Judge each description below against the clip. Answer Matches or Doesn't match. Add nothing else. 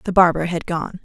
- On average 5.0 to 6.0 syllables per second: Matches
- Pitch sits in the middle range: Matches